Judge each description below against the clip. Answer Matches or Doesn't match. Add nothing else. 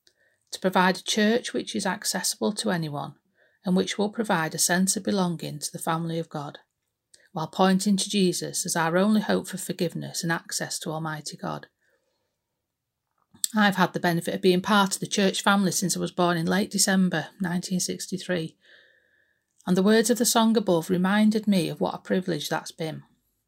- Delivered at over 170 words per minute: Matches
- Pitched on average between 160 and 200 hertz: Matches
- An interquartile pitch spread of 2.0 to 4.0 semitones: Matches